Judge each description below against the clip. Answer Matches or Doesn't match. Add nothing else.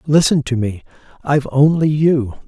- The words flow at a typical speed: Matches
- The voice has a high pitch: Doesn't match